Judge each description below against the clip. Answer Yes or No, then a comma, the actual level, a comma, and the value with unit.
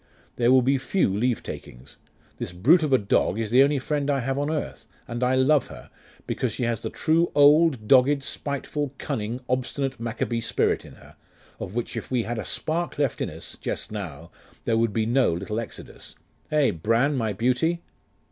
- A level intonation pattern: No, average, 4.1 semitones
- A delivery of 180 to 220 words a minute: Yes, average, 190 wpm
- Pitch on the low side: Yes, low, 125 Hz